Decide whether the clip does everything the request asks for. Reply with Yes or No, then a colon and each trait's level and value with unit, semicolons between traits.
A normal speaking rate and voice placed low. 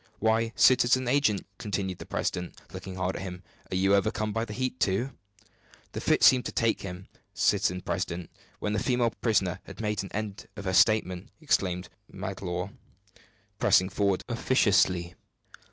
Yes: average, 155 wpm; low, 100 Hz